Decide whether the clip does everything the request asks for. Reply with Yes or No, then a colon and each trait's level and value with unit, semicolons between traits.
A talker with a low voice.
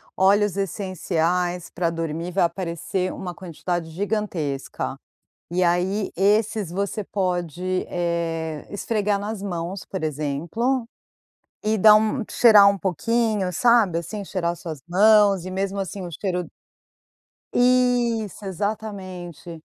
No: medium, 185 Hz